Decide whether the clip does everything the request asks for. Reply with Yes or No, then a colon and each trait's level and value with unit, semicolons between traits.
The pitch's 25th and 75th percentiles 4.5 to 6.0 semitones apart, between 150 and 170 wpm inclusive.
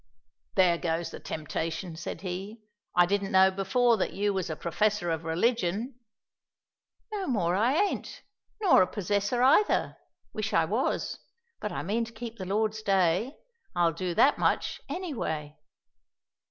Yes: average, 4.8 semitones; average, 155 wpm